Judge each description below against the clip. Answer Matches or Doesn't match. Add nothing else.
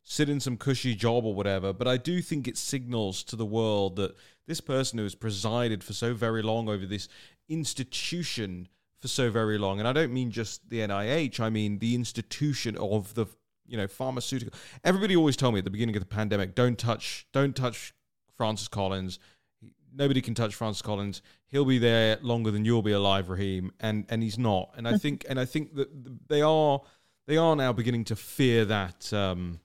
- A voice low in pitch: Matches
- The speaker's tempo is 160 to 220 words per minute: Matches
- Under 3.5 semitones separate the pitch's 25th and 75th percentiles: Doesn't match